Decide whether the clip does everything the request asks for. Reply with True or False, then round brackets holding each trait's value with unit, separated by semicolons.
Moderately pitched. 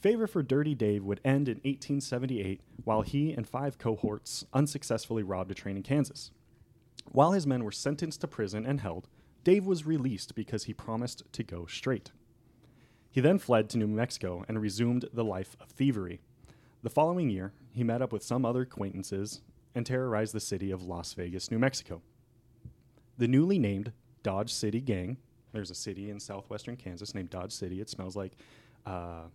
False (115 Hz)